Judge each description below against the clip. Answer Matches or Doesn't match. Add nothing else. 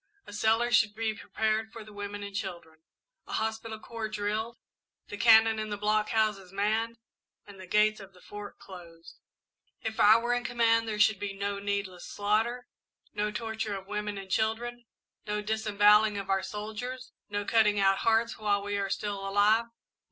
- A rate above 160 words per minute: Matches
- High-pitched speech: Matches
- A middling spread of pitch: Doesn't match